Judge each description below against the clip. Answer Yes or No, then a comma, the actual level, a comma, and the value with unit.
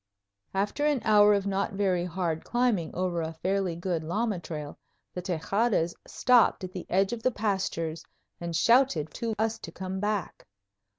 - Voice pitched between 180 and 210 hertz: Yes, high, 190 Hz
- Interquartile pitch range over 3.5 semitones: Yes, average, 3.9 semitones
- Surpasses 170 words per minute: No, average, 165 wpm